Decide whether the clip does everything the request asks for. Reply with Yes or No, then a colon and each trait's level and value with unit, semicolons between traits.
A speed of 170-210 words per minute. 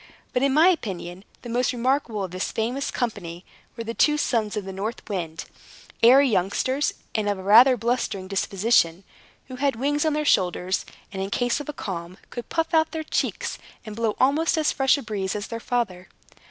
Yes: average, 195 wpm